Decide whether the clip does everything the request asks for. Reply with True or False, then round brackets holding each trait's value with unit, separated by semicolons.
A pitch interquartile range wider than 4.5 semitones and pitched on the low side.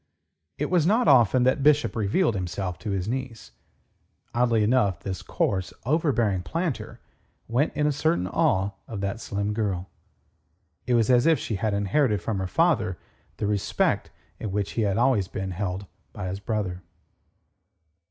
True (5.1 semitones; 110 Hz)